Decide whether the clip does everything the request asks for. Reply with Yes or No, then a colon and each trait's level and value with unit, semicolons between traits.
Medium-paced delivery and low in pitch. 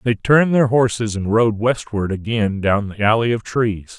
Yes: average, 195 wpm; low, 110 Hz